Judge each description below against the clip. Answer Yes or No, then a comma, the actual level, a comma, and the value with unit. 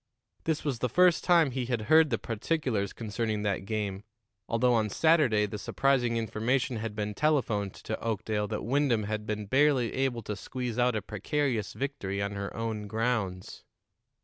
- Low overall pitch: Yes, low, 115 Hz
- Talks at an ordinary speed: Yes, average, 170 wpm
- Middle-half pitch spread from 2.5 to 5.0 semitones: Yes, average, 4.0 semitones